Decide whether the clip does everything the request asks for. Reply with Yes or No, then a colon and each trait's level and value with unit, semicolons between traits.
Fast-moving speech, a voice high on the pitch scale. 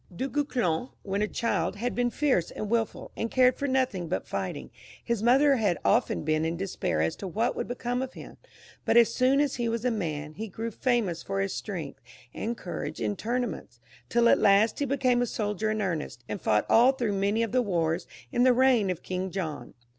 Yes: fast, 215 wpm; high, 225 Hz